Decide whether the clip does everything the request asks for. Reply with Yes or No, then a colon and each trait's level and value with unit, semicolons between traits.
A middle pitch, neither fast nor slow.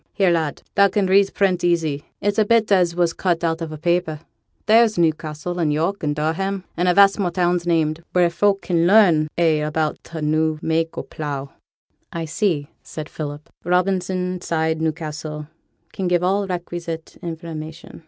Yes: medium, 170 Hz; average, 175 wpm